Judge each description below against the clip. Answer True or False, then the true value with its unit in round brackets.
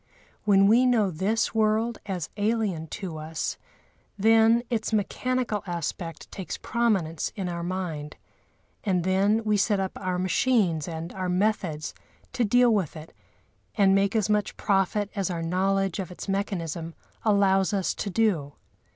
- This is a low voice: False (195 Hz)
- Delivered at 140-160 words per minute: True (150 wpm)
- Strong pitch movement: False (3.5 semitones)